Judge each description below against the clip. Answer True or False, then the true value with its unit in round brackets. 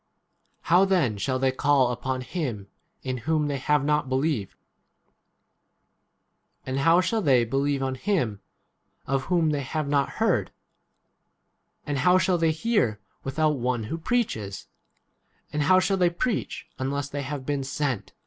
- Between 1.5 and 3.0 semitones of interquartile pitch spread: False (3.9 semitones)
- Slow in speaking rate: False (150 wpm)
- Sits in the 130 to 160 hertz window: True (140 Hz)